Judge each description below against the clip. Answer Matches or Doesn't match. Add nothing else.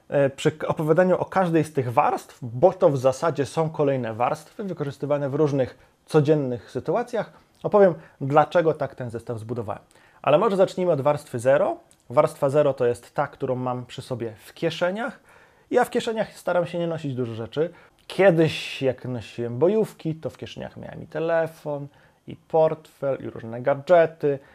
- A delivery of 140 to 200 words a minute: Matches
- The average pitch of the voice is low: Doesn't match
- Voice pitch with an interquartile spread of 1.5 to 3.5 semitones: Doesn't match